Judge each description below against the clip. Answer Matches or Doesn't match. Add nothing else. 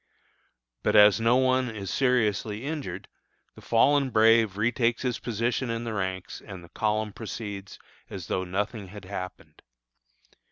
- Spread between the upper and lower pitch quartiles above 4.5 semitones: Doesn't match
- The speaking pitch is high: Doesn't match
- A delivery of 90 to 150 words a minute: Matches